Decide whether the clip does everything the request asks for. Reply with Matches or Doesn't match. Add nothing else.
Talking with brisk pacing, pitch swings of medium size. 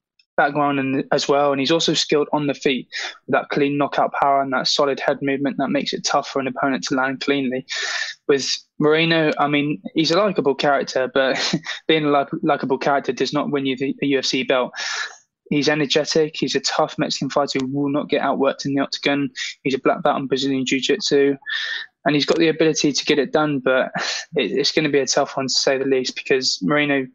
Doesn't match